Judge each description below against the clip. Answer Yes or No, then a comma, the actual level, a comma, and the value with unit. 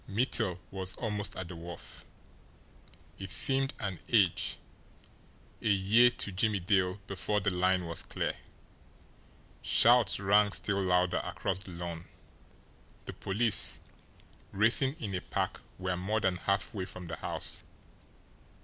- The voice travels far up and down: No, average, 2.7 semitones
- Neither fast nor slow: No, slow, 130 wpm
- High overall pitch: No, very low, 95 Hz